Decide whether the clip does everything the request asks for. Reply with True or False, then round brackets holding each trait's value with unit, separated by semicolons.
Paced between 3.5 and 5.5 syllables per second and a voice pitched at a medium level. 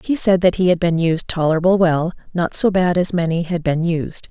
True (5.3 syllables/s; 175 Hz)